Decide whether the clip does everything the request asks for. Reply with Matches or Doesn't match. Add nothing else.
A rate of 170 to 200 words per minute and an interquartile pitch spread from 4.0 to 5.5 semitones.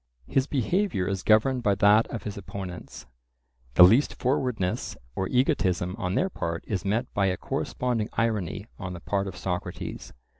Doesn't match